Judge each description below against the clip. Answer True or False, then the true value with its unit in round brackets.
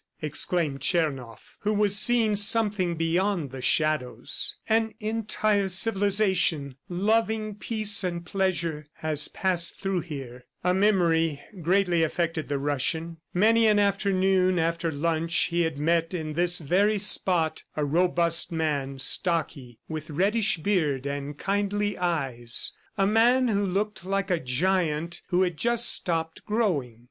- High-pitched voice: False (175 Hz)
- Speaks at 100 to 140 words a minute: True (135 wpm)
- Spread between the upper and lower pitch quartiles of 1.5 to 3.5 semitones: False (4.6 semitones)